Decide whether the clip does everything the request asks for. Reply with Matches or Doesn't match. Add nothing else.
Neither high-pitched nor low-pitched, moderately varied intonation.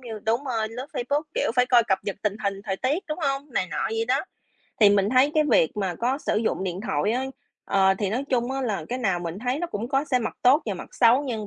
Doesn't match